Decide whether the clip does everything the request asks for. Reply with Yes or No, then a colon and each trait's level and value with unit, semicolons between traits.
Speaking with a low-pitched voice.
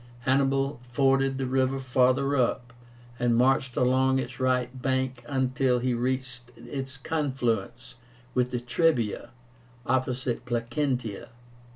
Yes: low, 130 Hz